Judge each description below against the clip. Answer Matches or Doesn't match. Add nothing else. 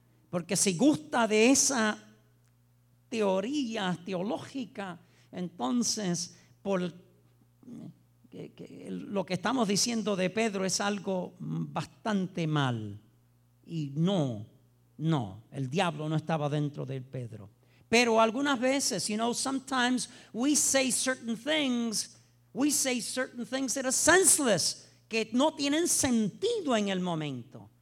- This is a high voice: Matches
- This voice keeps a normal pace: Doesn't match